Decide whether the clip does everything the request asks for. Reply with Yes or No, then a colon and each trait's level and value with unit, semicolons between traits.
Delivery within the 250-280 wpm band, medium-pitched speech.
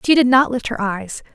No: fast, 270 wpm; high, 240 Hz